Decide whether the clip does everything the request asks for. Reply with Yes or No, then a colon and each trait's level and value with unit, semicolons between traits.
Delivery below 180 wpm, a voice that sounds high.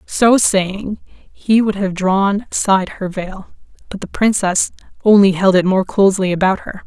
Yes: average, 165 wpm; high, 195 Hz